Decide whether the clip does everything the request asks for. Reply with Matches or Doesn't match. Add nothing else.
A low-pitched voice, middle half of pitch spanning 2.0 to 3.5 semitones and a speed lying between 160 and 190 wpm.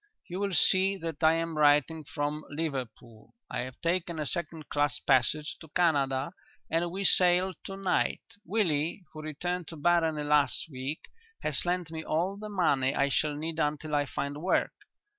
Doesn't match